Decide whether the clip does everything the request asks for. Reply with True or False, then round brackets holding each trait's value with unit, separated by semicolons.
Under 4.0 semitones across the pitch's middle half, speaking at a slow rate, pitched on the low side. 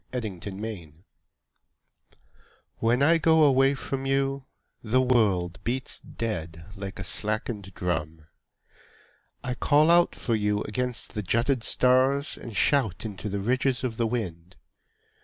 False (5.2 semitones; 130 wpm; 115 Hz)